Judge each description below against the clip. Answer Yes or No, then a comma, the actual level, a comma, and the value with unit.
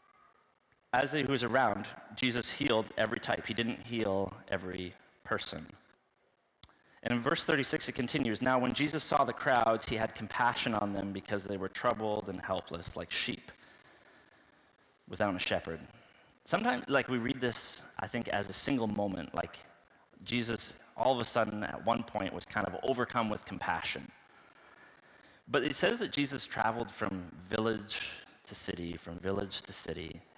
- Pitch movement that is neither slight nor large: Yes, average, 4.4 semitones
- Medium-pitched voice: No, low, 110 Hz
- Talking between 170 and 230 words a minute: No, average, 160 wpm